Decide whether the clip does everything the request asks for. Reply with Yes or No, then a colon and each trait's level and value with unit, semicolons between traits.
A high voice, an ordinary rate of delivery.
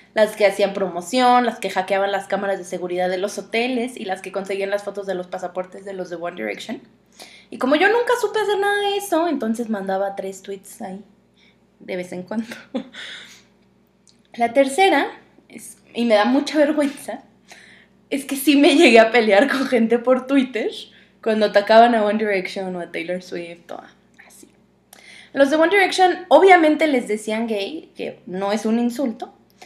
Yes: high, 225 Hz; average, 180 wpm